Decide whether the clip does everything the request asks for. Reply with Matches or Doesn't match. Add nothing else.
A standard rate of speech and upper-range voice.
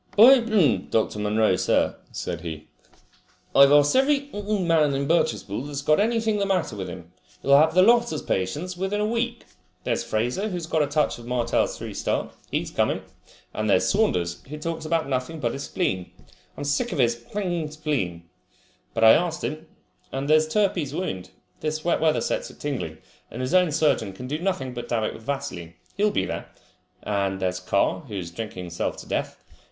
Doesn't match